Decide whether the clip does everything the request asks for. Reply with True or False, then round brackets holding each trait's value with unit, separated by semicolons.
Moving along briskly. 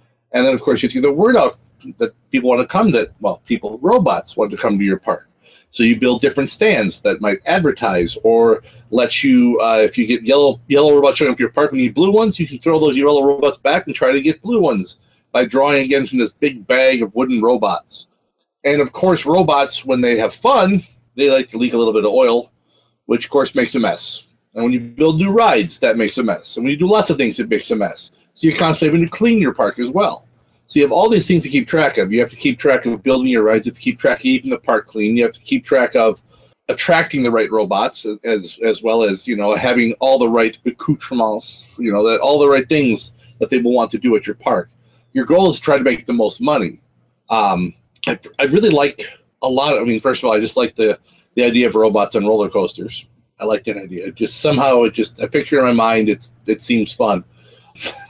True (255 wpm)